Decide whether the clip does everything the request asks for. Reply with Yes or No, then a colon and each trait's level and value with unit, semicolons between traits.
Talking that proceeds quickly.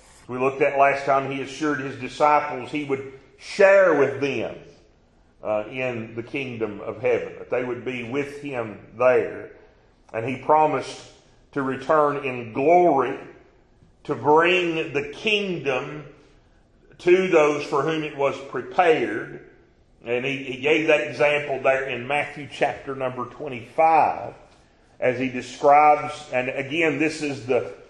No: average, 140 wpm